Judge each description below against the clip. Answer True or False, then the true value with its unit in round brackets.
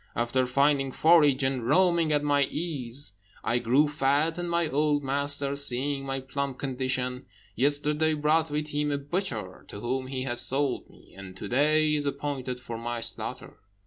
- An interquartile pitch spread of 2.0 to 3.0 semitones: True (2.6 semitones)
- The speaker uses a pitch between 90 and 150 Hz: True (140 Hz)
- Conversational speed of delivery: True (170 wpm)